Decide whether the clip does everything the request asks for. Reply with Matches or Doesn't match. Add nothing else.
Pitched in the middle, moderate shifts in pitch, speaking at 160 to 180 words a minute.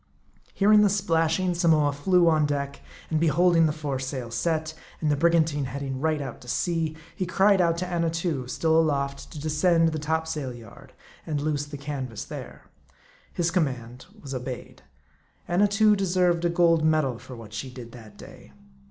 Matches